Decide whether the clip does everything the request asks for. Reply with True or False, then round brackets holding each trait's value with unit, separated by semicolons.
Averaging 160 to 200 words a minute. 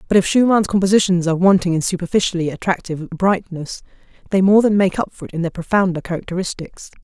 True (180 wpm)